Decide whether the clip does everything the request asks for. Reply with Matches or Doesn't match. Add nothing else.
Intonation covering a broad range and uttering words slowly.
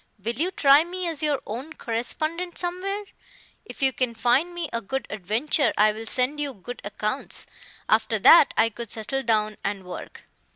Doesn't match